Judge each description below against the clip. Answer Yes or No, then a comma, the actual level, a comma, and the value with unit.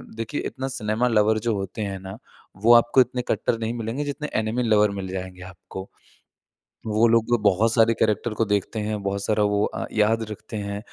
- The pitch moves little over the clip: Yes, narrow, 2.2 semitones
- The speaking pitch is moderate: No, low, 110 Hz